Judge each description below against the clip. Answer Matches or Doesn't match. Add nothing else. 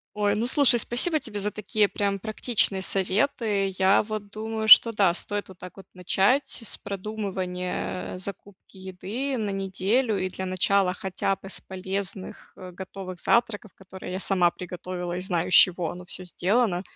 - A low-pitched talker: Doesn't match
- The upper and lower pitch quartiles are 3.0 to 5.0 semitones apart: Doesn't match